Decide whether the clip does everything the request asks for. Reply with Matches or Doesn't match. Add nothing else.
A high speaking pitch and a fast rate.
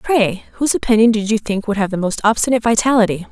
Matches